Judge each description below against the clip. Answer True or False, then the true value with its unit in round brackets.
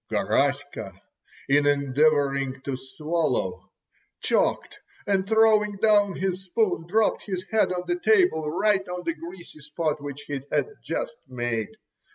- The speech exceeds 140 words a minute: False (135 wpm)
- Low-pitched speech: False (170 Hz)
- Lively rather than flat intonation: True (6.1 semitones)